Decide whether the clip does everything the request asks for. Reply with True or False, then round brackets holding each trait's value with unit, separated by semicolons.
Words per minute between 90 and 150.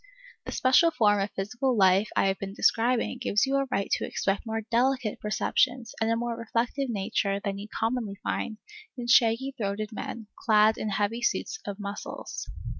False (180 wpm)